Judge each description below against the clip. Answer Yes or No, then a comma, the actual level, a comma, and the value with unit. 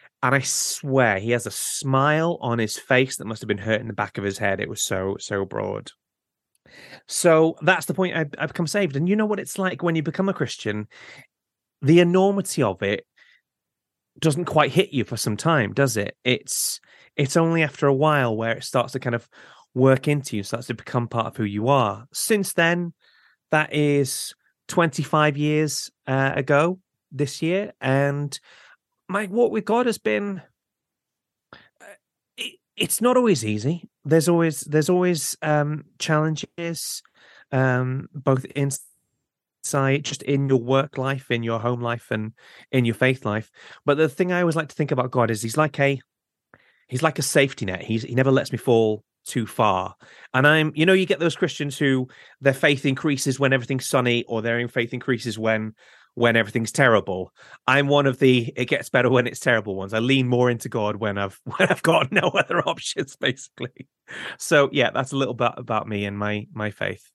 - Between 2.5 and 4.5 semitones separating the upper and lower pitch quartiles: No, average, 5.1 semitones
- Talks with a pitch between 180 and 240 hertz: No, low, 135 Hz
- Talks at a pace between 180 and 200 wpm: Yes, average, 190 wpm